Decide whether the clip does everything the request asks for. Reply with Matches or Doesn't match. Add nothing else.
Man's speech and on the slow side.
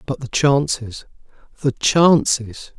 Matches